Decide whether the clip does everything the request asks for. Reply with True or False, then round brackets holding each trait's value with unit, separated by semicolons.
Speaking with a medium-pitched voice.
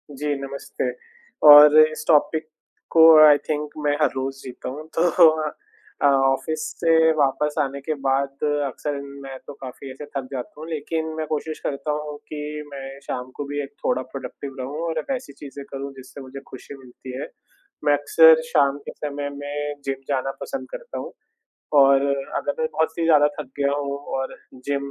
True (145 Hz)